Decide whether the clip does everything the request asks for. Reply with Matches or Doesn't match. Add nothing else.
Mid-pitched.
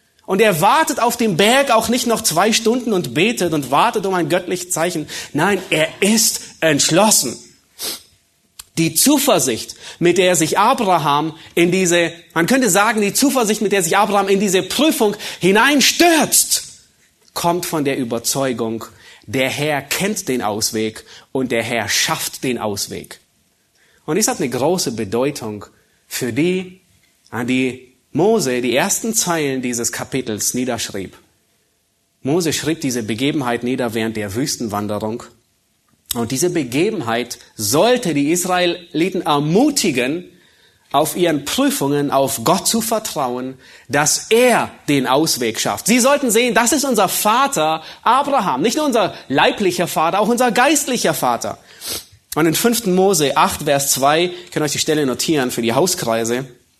Matches